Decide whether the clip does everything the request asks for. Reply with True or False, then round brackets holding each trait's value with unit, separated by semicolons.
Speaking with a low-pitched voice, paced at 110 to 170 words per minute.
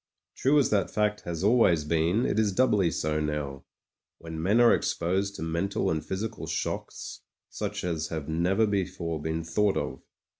True (90 Hz; 165 wpm)